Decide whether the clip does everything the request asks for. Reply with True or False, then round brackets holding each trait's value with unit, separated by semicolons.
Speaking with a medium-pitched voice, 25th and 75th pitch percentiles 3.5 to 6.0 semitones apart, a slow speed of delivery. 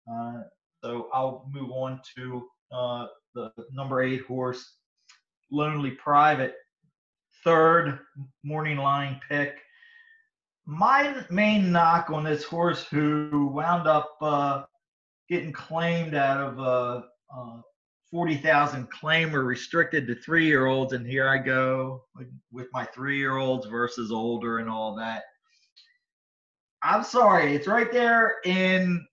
True (145 Hz; 4.6 semitones; 125 wpm)